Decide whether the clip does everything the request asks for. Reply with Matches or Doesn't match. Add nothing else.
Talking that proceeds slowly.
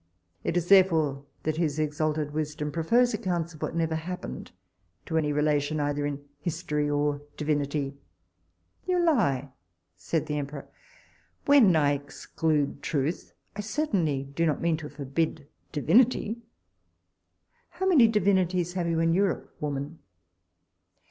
Matches